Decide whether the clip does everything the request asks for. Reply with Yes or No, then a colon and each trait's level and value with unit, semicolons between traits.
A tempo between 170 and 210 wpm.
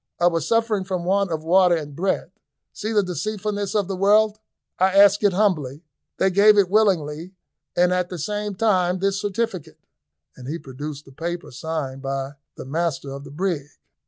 Yes: average, 180 wpm